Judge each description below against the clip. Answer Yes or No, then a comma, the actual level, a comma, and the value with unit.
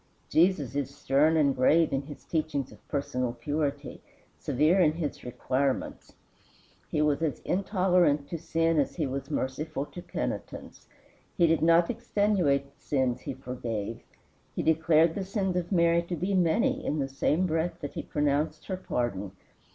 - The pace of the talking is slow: No, average, 160 wpm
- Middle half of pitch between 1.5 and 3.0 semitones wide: No, average, 3.7 semitones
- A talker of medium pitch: Yes, medium, 155 Hz